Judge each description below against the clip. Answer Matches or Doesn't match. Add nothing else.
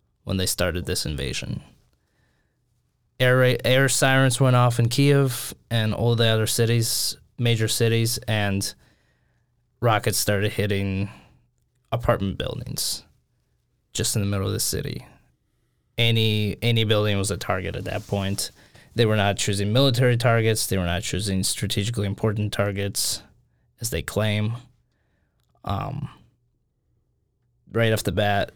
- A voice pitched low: Matches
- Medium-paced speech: Doesn't match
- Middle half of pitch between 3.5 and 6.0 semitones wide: Doesn't match